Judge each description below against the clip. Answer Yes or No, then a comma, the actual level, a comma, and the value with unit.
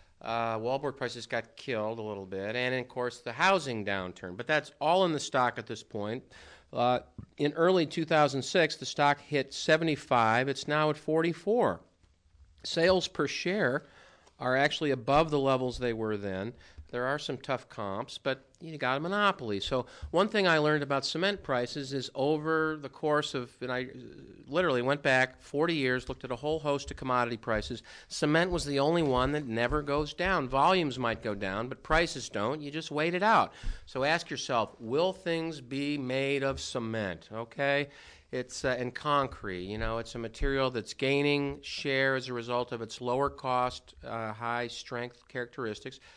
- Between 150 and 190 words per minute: Yes, average, 180 wpm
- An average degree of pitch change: Yes, average, 4.0 semitones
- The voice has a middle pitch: No, low, 130 Hz